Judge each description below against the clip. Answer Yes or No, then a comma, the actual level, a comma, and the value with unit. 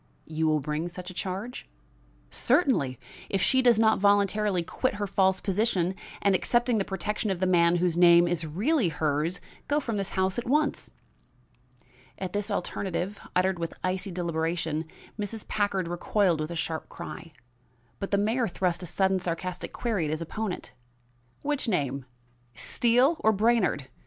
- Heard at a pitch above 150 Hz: Yes, high, 190 Hz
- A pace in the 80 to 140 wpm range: No, average, 160 wpm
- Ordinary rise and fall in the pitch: Yes, average, 3.9 semitones